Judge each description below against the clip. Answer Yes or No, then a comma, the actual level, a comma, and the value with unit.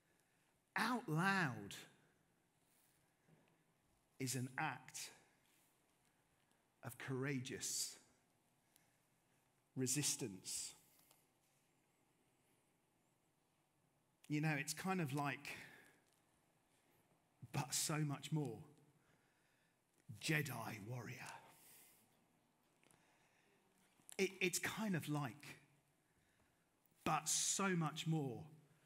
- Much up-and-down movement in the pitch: No, average, 2.7 semitones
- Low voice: No, medium, 150 Hz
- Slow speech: Yes, slow, 60 wpm